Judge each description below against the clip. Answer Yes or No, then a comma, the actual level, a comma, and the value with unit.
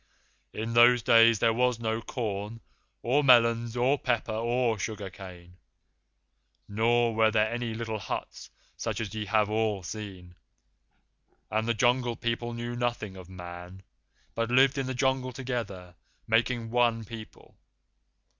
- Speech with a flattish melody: Yes, narrow, 2.2 semitones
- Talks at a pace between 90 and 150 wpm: Yes, average, 140 wpm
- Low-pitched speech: Yes, low, 115 Hz